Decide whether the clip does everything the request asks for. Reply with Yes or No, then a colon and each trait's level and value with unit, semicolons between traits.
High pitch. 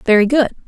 Yes: high, 240 Hz